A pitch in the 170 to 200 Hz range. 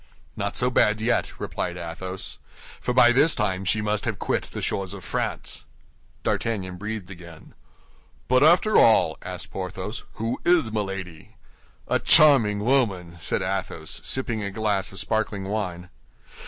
No: low, 105 Hz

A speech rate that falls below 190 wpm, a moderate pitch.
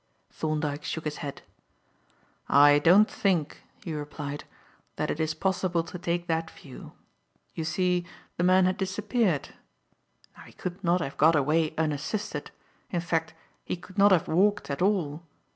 Yes: average, 155 wpm; medium, 165 Hz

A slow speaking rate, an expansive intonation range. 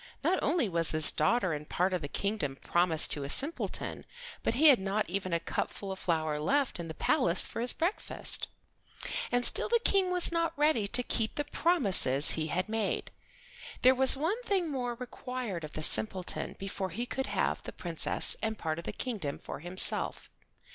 No: average, 190 wpm; wide, 7.8 semitones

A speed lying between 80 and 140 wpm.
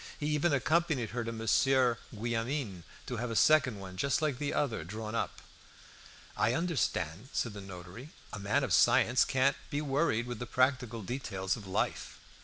No: average, 175 wpm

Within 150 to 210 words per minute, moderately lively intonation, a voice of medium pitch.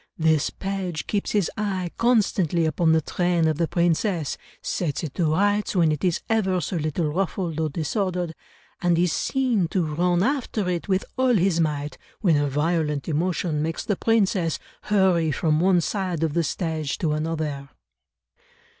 Yes: average, 165 wpm; average, 3.3 semitones; medium, 170 Hz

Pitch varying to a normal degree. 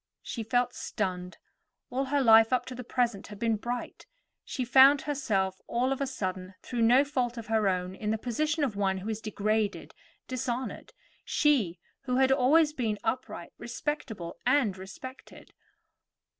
Yes: average, 4.0 semitones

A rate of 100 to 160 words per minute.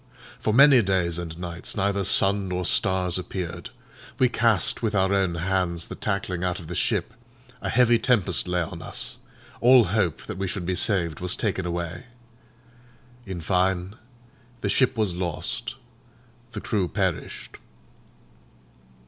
Yes: average, 150 wpm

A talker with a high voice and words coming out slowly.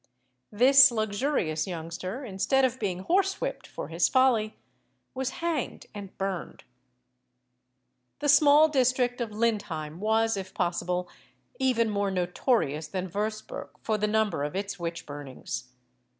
Yes: high, 210 Hz; slow, 125 wpm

